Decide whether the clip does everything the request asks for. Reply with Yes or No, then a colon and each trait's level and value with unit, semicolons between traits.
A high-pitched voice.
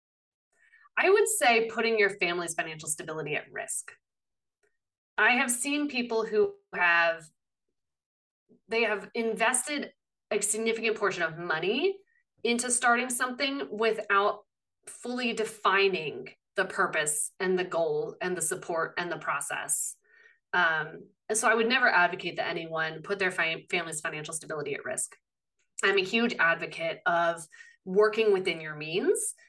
Yes: high, 215 Hz